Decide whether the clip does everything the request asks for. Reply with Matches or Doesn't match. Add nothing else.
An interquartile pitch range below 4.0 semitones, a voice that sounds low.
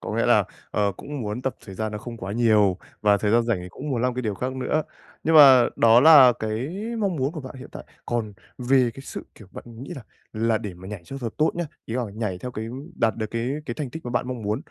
Matches